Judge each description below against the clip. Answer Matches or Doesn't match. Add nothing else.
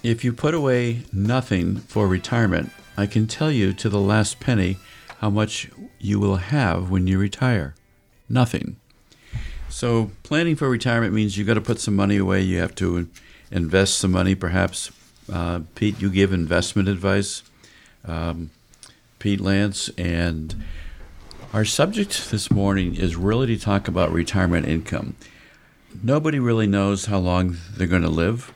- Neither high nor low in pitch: Doesn't match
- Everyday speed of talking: Matches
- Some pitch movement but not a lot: Matches